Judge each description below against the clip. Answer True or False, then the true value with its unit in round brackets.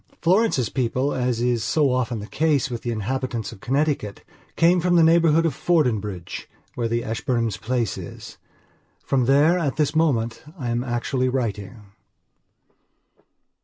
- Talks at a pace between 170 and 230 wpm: False (145 wpm)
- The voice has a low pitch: True (125 Hz)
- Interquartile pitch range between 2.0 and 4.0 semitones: False (4.6 semitones)